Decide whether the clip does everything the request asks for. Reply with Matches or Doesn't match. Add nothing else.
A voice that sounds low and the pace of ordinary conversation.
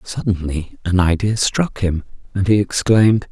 Matches